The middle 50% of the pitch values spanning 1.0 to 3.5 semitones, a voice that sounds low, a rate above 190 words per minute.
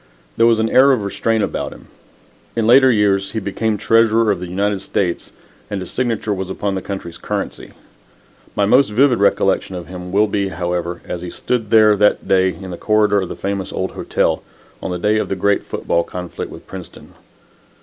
Yes: average, 2.9 semitones; low, 100 Hz; average, 200 wpm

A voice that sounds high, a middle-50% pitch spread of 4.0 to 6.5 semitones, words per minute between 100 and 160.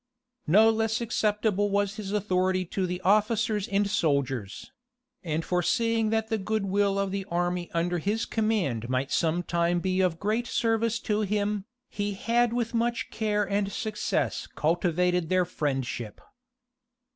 No: high, 200 Hz; average, 3.5 semitones; average, 145 wpm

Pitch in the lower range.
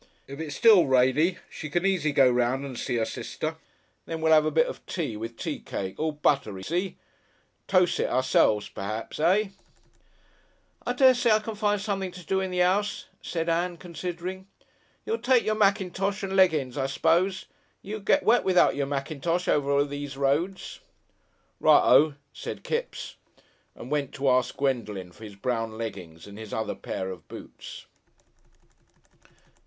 No: medium, 155 Hz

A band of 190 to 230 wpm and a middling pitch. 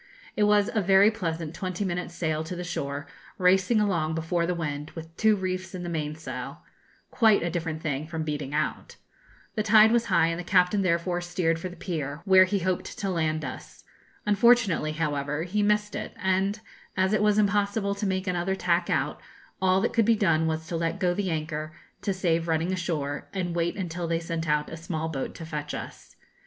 Yes: average, 200 wpm; medium, 175 Hz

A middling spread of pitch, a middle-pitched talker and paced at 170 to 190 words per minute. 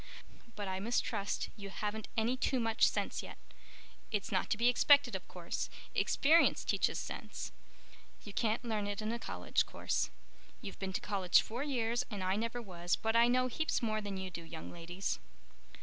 No: average, 3.5 semitones; high, 215 Hz; average, 180 wpm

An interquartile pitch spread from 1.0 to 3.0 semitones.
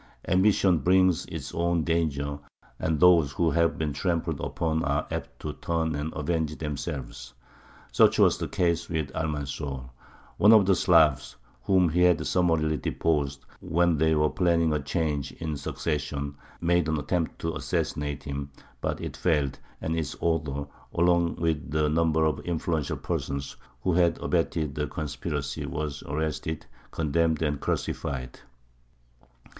Yes: narrow, 2.6 semitones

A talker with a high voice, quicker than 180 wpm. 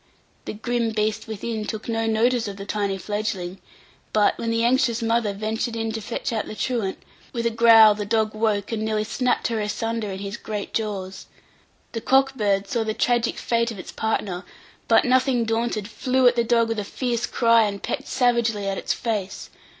Yes: high, 225 Hz; average, 195 wpm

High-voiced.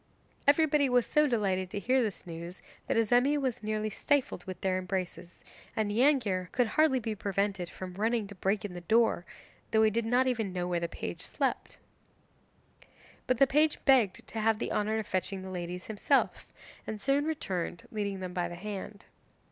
Yes: high, 210 Hz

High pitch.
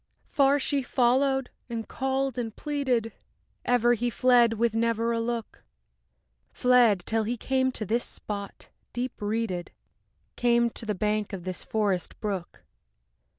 Yes: high, 235 Hz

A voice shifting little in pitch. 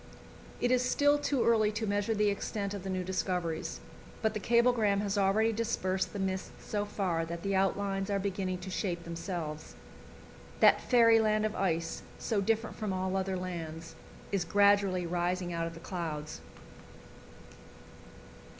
No: average, 3.1 semitones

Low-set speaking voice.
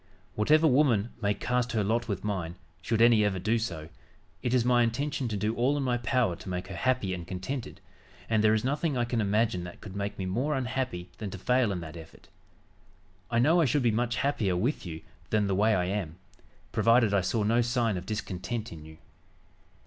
Yes: low, 110 Hz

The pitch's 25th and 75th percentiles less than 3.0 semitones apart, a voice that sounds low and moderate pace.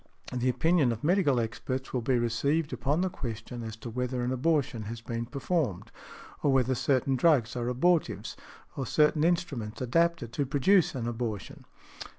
No: average, 4.3 semitones; low, 130 Hz; average, 165 wpm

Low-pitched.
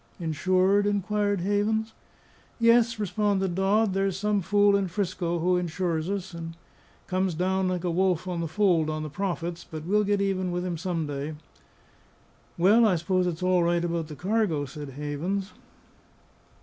No: medium, 185 Hz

